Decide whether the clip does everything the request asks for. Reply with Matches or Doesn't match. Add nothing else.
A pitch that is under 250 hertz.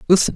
Matches